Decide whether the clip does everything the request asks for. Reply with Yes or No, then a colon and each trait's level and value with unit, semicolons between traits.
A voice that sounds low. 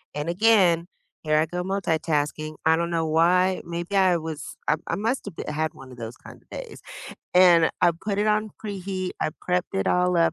No: medium, 170 Hz